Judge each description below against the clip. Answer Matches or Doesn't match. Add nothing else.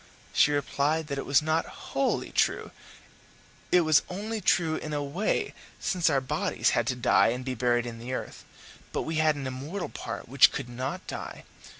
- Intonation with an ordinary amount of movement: Matches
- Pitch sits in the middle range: Matches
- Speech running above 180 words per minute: Matches